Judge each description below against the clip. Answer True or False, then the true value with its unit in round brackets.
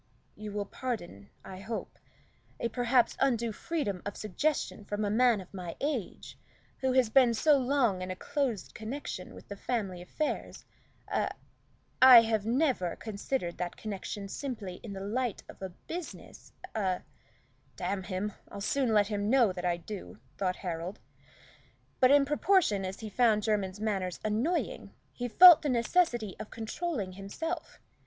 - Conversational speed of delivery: True (155 wpm)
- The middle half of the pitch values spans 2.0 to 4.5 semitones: False (4.9 semitones)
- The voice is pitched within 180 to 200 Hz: False (215 Hz)